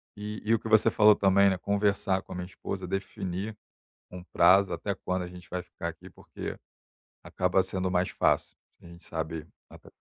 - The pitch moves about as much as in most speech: No, narrow, 1.9 semitones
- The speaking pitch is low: Yes, very low, 95 Hz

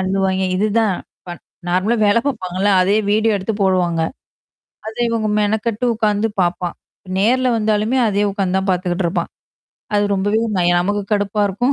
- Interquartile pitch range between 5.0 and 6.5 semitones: No, narrow, 2.6 semitones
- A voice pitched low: No, high, 205 Hz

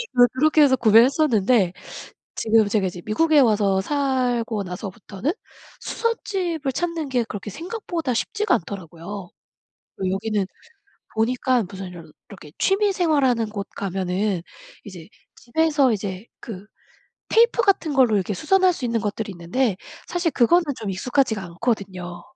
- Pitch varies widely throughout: Yes, wide, 7.1 semitones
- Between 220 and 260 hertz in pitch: Yes, high, 225 Hz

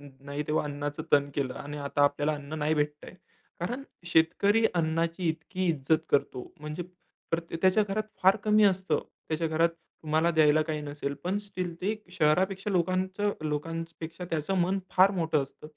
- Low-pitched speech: No, medium, 165 Hz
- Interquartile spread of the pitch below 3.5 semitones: No, average, 3.8 semitones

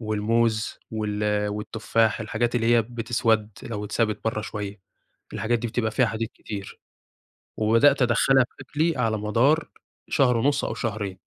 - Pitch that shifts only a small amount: Yes, narrow, 2.0 semitones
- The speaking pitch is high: No, low, 110 Hz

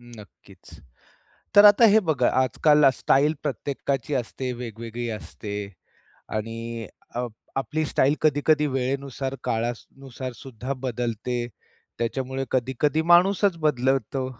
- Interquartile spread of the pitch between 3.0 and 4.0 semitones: Yes, average, 3.6 semitones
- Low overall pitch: Yes, low, 130 Hz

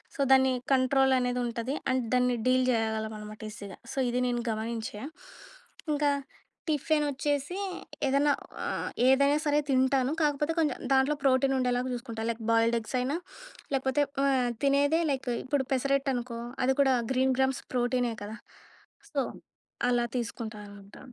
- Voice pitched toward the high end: Yes, very high, 260 Hz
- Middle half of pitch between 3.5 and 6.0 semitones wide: No, average, 2.7 semitones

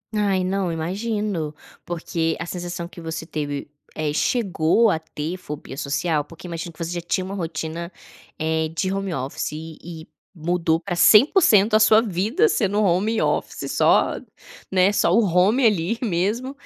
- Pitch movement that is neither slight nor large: Yes, average, 4.0 semitones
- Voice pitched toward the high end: No, medium, 175 Hz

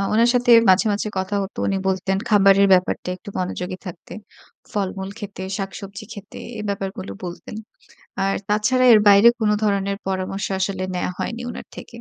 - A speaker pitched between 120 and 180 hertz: No, high, 195 Hz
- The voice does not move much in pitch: Yes, narrow, 1.7 semitones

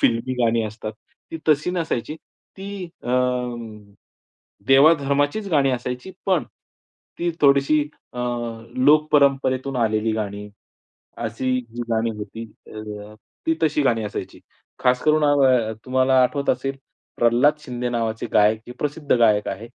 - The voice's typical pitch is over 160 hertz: No, low, 130 Hz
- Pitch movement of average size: Yes, average, 4.3 semitones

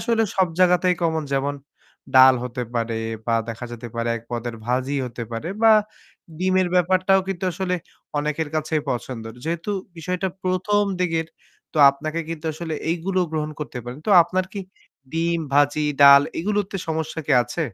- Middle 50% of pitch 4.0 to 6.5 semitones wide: Yes, average, 5.2 semitones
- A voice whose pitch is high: No, medium, 160 Hz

